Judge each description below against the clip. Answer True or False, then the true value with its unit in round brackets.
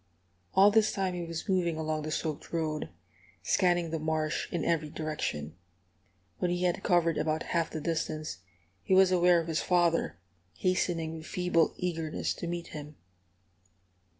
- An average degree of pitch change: False (2.3 semitones)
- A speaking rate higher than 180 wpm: False (155 wpm)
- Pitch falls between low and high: True (165 Hz)